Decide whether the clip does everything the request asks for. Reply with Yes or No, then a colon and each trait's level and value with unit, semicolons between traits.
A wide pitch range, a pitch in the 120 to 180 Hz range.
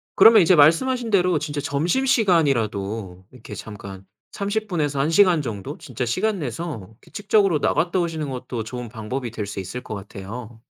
Yes: wide, 8.2 semitones; medium, 140 Hz